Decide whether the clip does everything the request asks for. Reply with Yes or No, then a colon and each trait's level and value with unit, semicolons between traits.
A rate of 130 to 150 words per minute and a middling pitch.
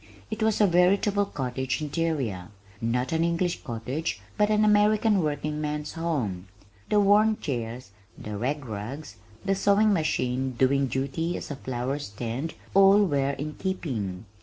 Yes: average, 140 wpm; medium, 150 Hz